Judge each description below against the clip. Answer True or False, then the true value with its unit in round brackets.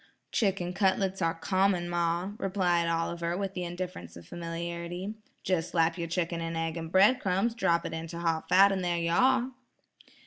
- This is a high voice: False (175 Hz)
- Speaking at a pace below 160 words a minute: False (175 wpm)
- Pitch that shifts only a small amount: True (2.3 semitones)